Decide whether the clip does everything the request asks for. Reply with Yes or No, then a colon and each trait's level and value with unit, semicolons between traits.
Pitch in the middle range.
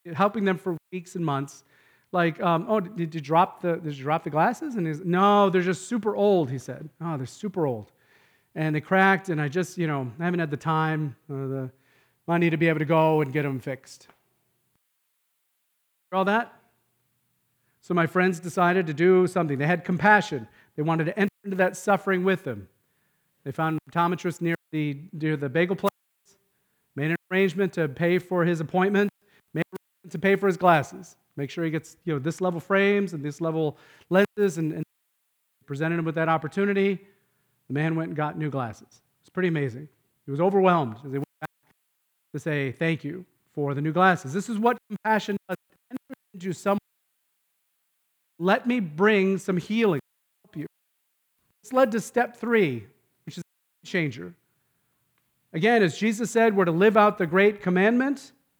Yes: medium, 170 Hz